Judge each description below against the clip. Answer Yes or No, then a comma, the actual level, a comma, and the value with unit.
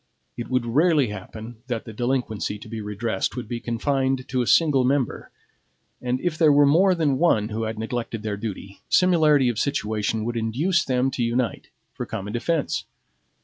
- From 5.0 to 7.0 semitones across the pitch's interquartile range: No, average, 4.1 semitones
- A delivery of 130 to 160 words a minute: No, average, 180 wpm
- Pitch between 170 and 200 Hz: No, low, 120 Hz